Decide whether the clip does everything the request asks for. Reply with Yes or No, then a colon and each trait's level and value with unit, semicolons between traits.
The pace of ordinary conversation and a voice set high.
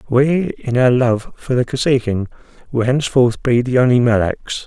No: average, 165 wpm; low, 125 Hz